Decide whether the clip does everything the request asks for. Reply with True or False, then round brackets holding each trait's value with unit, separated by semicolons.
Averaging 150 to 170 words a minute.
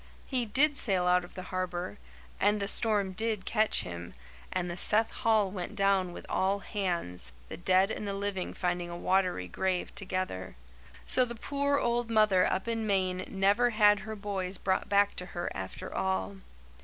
False (180 wpm)